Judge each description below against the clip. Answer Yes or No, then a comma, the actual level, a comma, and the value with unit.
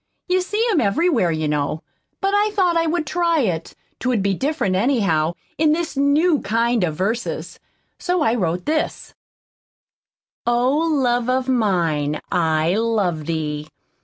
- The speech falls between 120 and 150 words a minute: Yes, average, 145 wpm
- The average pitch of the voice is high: Yes, high, 235 Hz